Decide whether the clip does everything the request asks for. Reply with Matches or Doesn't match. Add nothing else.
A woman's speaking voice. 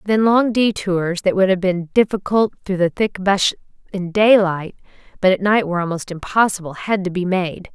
Matches